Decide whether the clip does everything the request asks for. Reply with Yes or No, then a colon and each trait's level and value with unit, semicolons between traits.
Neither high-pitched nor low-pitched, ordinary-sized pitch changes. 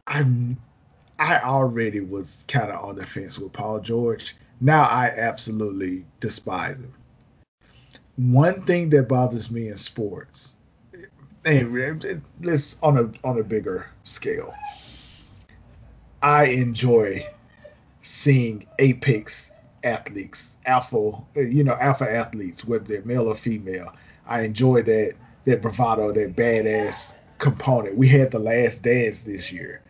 No: low, 120 Hz; average, 3.4 semitones